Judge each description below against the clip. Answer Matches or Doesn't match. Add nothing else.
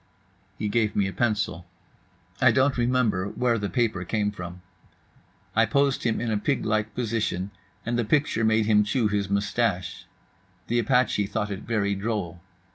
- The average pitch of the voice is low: Matches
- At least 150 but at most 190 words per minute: Matches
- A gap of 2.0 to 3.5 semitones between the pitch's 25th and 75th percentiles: Matches